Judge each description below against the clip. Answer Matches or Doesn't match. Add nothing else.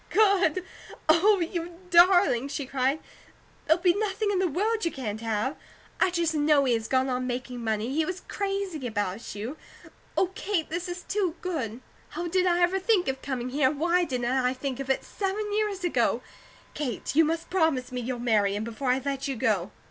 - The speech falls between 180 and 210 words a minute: Matches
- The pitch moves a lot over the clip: Matches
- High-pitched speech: Matches